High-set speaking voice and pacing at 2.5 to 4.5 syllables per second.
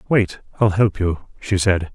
No: low, 100 Hz; 4.1 syllables/s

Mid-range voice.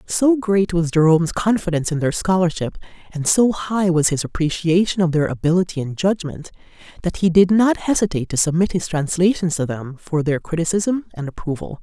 Yes: medium, 175 Hz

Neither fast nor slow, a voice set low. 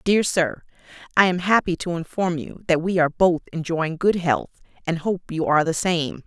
No: average, 190 wpm; medium, 170 Hz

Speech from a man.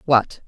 No: female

